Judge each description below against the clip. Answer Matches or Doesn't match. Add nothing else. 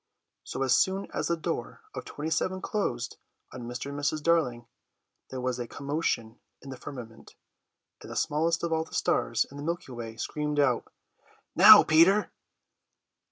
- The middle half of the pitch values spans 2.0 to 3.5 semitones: Doesn't match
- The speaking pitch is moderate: Matches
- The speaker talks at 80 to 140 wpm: Doesn't match